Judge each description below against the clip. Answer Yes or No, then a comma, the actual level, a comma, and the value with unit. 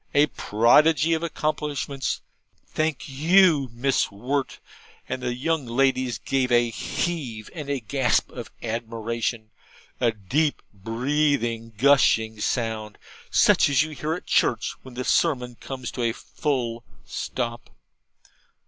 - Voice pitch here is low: Yes, low, 130 Hz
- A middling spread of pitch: Yes, average, 3.9 semitones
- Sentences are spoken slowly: Yes, slow, 125 wpm